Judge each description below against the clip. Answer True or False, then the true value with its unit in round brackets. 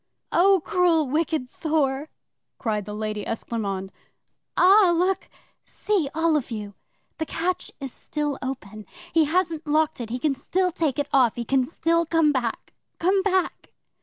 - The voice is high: True (300 Hz)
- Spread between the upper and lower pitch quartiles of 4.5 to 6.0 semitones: True (5.5 semitones)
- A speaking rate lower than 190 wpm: True (155 wpm)